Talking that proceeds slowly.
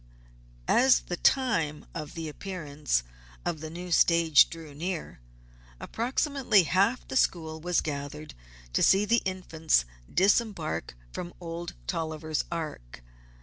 Yes: slow, 115 wpm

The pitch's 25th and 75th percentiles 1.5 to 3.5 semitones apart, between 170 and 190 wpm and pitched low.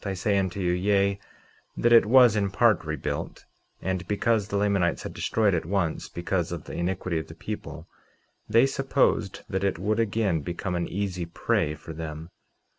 Yes: average, 3.1 semitones; average, 180 wpm; very low, 95 Hz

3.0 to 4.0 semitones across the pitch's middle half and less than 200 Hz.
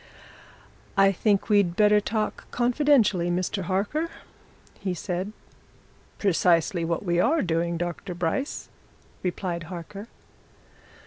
Yes: average, 3.4 semitones; high, 190 Hz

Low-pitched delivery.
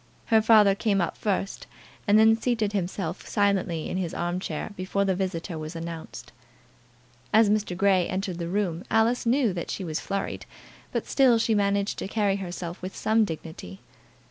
No: high, 195 Hz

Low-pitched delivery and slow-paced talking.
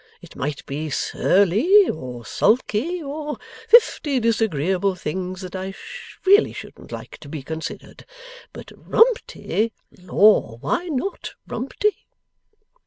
No: high, 205 Hz; slow, 110 wpm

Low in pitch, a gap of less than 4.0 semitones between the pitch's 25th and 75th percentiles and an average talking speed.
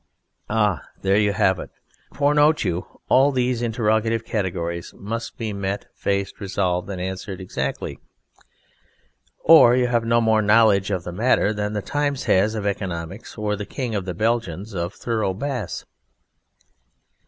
Yes: low, 105 Hz; average, 3.4 semitones; average, 155 wpm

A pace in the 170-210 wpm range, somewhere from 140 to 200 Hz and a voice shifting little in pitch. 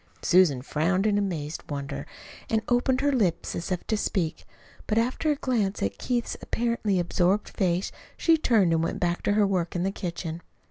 No: average, 185 wpm; high, 190 Hz; average, 4.7 semitones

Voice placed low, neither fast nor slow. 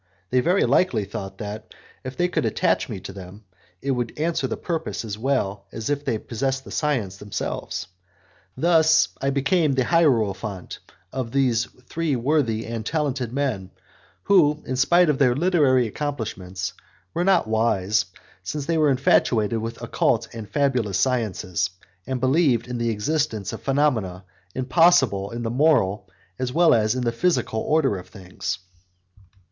Yes: low, 125 Hz; average, 155 wpm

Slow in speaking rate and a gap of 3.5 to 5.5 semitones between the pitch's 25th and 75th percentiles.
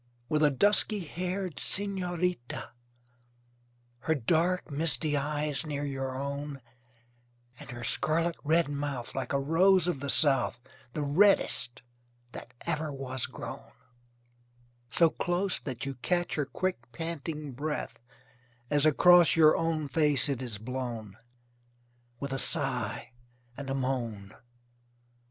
Yes: slow, 125 wpm; average, 3.8 semitones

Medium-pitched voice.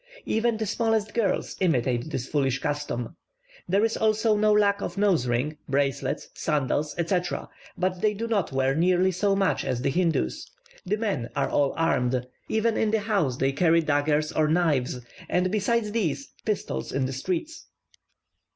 Yes: medium, 175 Hz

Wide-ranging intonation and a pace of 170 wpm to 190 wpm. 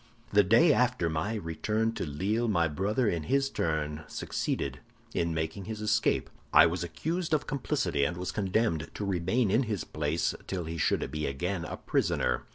Yes: wide, 5.7 semitones; average, 175 wpm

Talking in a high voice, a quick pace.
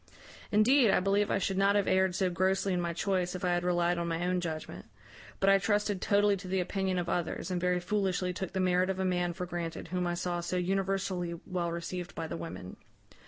No: medium, 180 Hz; fast, 230 wpm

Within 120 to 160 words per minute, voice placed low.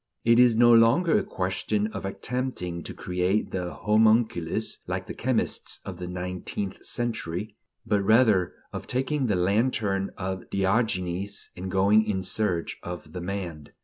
Yes: average, 145 wpm; low, 100 Hz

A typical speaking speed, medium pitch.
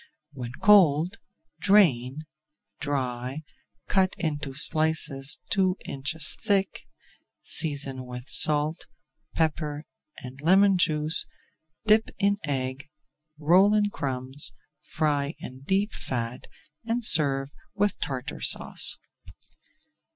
No: slow, 95 wpm; medium, 150 Hz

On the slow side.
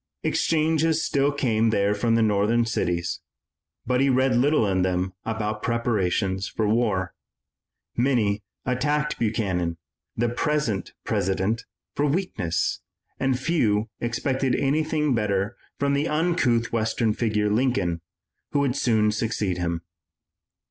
Yes: slow, 120 wpm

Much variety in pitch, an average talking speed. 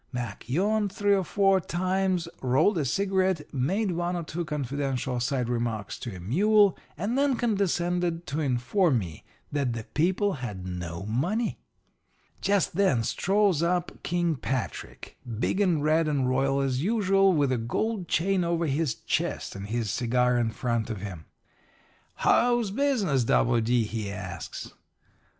Yes: wide, 7.9 semitones; average, 150 wpm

